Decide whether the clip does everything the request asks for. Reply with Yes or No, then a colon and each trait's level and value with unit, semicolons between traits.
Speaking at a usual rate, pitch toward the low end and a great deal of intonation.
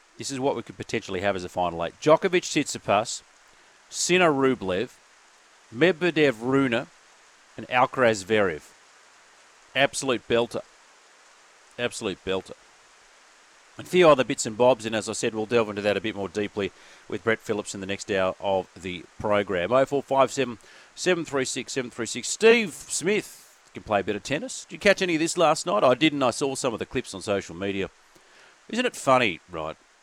Yes: average, 175 wpm; low, 120 Hz; wide, 6.0 semitones